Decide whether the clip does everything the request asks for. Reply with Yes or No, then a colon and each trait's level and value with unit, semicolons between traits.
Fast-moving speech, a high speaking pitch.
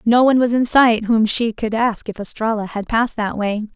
Yes: fast, 240 wpm; high, 225 Hz